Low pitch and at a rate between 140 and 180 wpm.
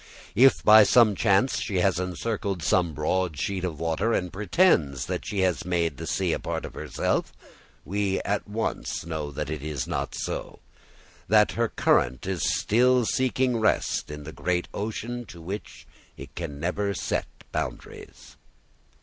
Yes: very low, 95 Hz; average, 160 wpm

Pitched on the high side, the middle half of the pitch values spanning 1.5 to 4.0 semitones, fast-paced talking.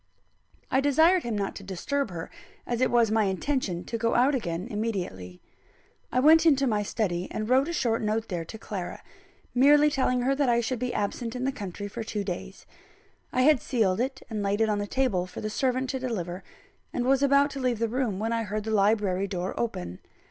No: high, 225 Hz; average, 4.5 semitones; fast, 215 wpm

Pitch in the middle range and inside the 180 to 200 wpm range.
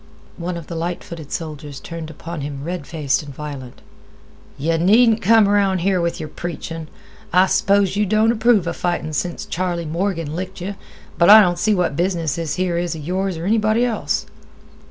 Yes: medium, 175 Hz; average, 190 wpm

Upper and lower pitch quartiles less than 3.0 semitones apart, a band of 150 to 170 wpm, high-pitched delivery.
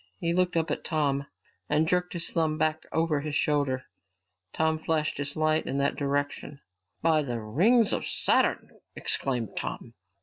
No: narrow, 2.5 semitones; average, 160 wpm; medium, 155 Hz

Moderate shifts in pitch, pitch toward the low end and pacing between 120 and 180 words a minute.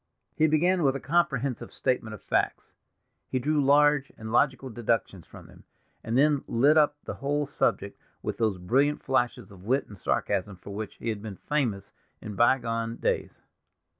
Yes: average, 4.8 semitones; low, 125 Hz; average, 170 wpm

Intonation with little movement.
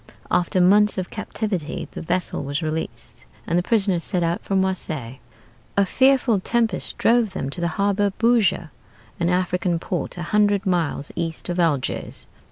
No: average, 3.3 semitones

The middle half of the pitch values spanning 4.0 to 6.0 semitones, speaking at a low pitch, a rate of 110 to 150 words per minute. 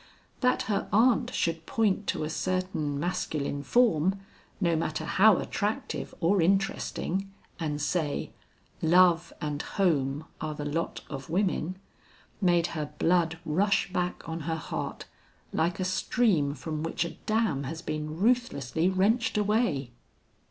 No: average, 4.3 semitones; medium, 170 Hz; slow, 135 wpm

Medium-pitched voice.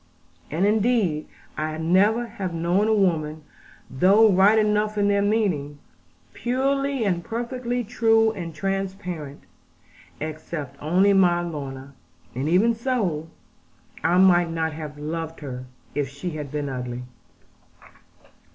Yes: medium, 180 Hz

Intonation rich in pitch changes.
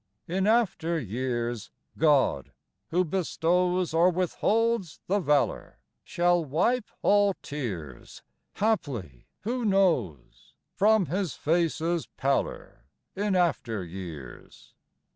Yes: wide, 7.1 semitones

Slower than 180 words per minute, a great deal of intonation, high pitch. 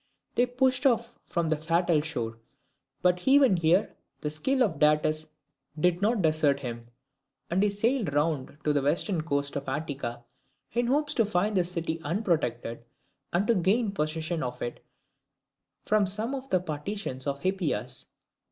No: average, 155 wpm; wide, 5.9 semitones; medium, 170 Hz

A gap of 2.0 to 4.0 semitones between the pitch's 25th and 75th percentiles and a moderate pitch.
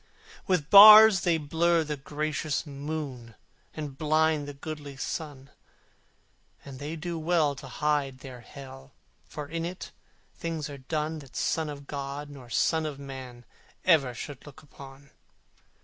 Yes: narrow, 2.5 semitones; medium, 145 Hz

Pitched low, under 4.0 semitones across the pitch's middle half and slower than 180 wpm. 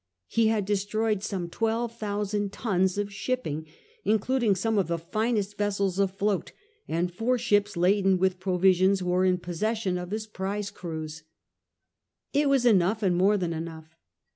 No: high, 200 Hz; average, 3.1 semitones; average, 155 wpm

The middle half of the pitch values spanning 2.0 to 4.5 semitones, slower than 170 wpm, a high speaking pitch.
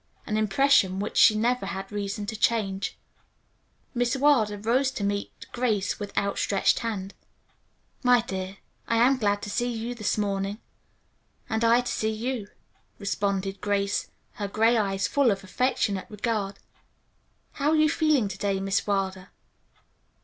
Yes: average, 3.3 semitones; average, 150 wpm; high, 210 Hz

